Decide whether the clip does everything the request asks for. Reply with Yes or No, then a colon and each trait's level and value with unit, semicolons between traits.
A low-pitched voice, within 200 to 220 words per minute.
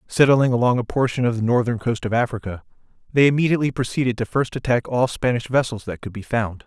Yes: low, 120 Hz; fast, 205 wpm